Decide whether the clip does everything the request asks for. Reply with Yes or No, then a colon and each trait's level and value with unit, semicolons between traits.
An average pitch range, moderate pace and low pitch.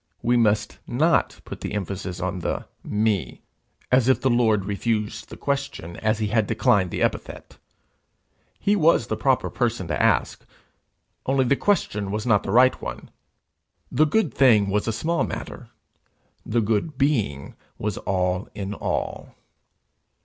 Yes: average, 4.5 semitones; average, 150 wpm; low, 110 Hz